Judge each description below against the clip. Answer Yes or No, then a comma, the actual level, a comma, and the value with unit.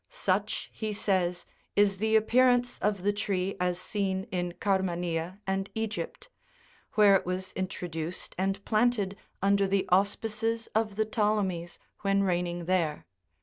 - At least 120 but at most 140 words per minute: Yes, slow, 135 wpm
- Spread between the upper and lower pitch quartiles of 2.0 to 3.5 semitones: Yes, average, 2.7 semitones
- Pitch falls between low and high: No, high, 195 Hz